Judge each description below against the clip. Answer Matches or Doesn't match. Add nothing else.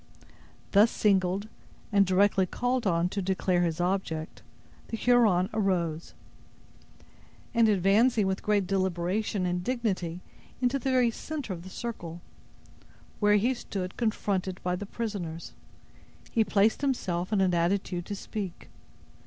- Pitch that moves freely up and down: Doesn't match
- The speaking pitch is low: Doesn't match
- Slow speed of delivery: Matches